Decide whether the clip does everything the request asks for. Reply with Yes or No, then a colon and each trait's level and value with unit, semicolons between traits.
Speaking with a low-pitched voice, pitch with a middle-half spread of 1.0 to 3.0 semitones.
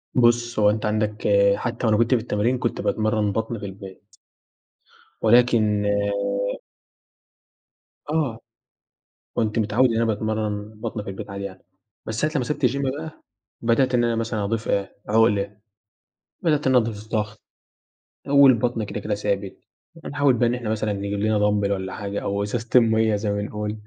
Yes: low, 110 Hz; narrow, 2.5 semitones